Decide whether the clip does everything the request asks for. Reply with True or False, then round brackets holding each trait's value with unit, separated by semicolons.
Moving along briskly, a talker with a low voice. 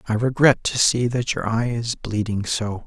True (210 wpm; 115 Hz)